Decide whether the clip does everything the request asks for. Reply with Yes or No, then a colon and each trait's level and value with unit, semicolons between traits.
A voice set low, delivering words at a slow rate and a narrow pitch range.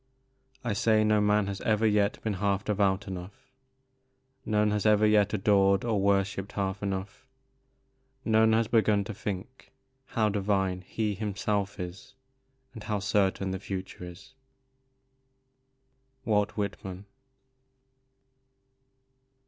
Yes: low, 100 Hz; slow, 115 wpm; narrow, 1.7 semitones